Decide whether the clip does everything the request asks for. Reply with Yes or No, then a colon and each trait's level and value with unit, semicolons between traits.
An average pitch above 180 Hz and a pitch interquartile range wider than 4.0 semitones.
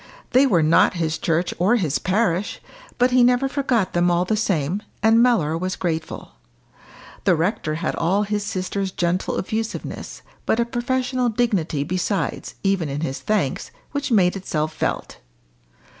Yes: high, 190 Hz; wide, 5.6 semitones